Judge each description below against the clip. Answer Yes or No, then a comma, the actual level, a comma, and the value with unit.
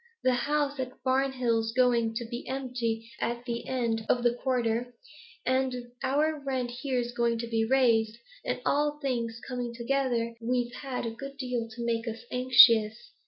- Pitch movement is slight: Yes, narrow, 2.0 semitones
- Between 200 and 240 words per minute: No, average, 165 wpm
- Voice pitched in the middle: No, high, 245 Hz